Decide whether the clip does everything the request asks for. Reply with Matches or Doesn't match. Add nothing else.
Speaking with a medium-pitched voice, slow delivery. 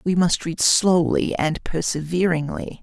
Matches